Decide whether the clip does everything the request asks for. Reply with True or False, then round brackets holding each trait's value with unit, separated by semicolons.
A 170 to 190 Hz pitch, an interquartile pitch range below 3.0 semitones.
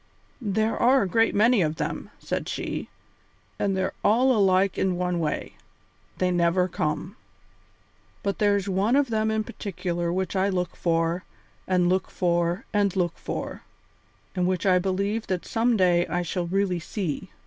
True (185 Hz; 2.6 semitones)